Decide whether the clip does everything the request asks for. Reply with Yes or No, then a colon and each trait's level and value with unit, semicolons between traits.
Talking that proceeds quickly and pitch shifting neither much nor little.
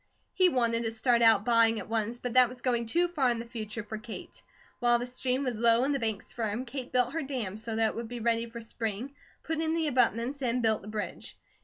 No: fast, 250 wpm; narrow, 2.1 semitones